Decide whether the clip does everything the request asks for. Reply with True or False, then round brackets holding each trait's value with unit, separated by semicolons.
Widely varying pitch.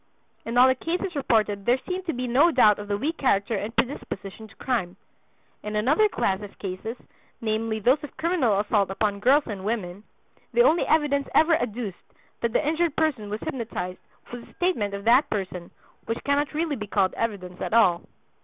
True (5.9 semitones)